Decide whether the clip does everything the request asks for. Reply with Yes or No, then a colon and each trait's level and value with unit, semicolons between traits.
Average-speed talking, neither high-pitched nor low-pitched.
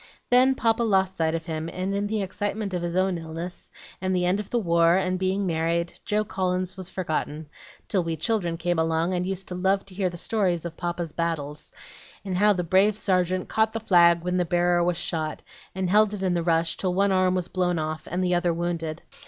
No: fast, 225 wpm; medium, 180 Hz